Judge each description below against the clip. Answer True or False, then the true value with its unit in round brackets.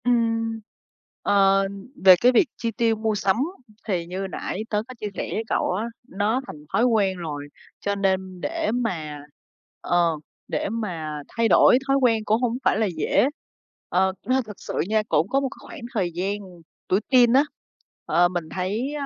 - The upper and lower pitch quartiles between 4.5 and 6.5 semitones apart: False (4.0 semitones)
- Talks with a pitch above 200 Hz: True (210 Hz)